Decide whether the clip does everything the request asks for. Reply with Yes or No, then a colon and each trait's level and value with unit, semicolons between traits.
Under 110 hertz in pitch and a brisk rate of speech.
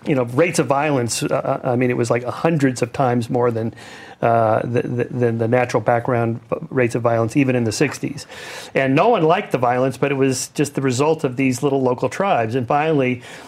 No: low, 130 Hz; fast, 220 wpm